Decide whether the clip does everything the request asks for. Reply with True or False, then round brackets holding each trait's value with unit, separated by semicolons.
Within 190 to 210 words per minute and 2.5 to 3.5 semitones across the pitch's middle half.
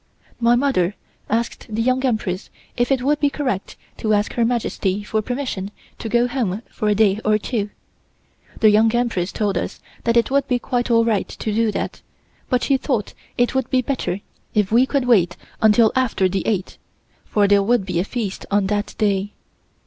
True (195 wpm; 3.2 semitones)